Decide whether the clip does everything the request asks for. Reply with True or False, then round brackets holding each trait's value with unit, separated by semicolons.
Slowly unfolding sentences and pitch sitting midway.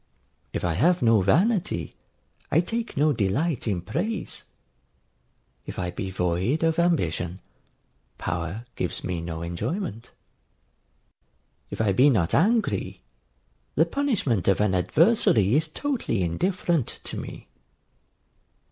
False (120 wpm; 115 Hz)